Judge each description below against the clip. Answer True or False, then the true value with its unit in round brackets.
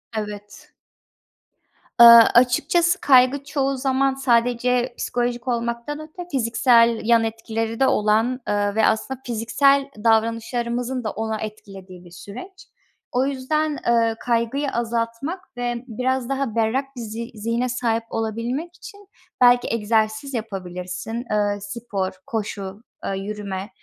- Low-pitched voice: False (235 Hz)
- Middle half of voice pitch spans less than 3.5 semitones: True (2.9 semitones)